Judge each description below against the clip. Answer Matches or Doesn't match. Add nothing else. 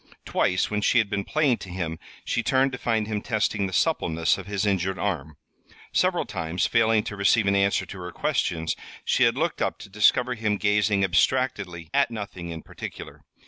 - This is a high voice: Doesn't match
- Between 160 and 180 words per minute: Doesn't match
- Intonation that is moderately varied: Matches